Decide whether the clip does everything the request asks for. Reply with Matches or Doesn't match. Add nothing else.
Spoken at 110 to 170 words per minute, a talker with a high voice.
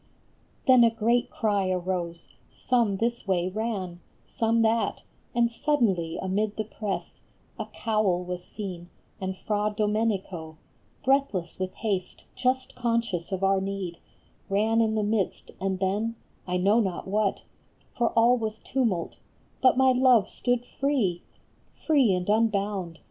Matches